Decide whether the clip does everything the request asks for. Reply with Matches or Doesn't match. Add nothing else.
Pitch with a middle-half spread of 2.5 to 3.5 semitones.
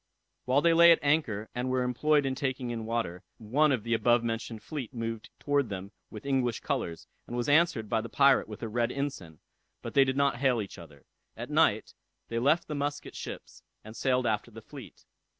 Doesn't match